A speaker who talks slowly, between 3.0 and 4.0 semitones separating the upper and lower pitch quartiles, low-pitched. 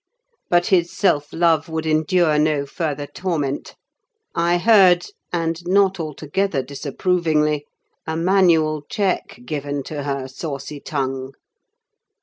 No: slow, 115 wpm; average, 3.4 semitones; medium, 155 Hz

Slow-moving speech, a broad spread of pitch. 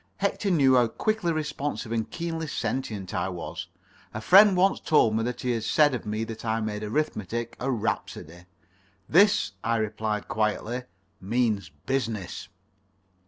No: average, 150 wpm; wide, 5.7 semitones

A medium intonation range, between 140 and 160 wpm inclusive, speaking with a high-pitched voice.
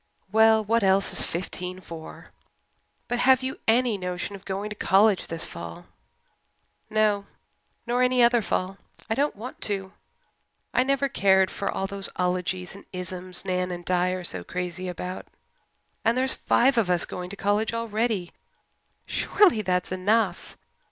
Yes: average, 3.8 semitones; average, 155 wpm; high, 195 Hz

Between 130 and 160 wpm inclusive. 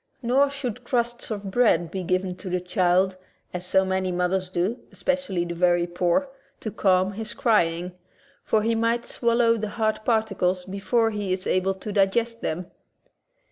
No: average, 175 wpm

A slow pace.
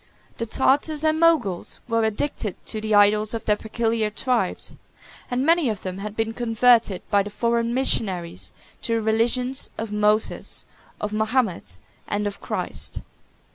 No: average, 150 wpm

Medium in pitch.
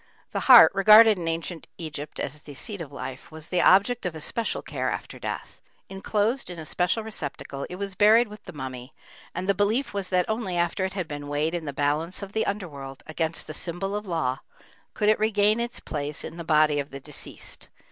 Yes: medium, 175 Hz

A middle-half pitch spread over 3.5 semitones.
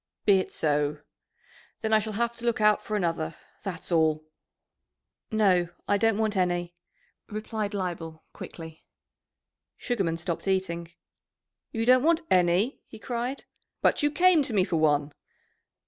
Yes: average, 4.9 semitones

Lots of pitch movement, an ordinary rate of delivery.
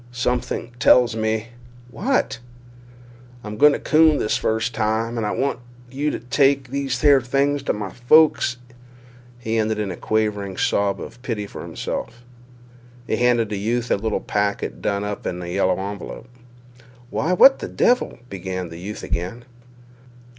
No: average, 4.0 semitones; average, 155 wpm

